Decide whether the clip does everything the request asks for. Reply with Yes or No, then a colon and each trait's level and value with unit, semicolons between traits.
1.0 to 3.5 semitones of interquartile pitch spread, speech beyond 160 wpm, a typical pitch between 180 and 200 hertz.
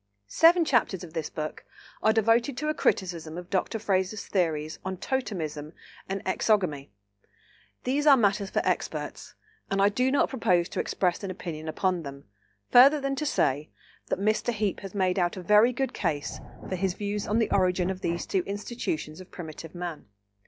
No: average, 4.5 semitones; average, 180 wpm; high, 190 Hz